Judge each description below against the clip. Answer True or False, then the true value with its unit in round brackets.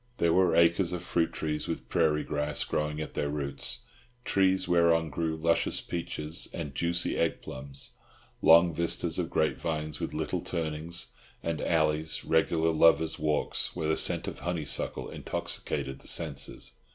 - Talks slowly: False (150 wpm)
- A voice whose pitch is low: True (80 Hz)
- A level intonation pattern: True (1.9 semitones)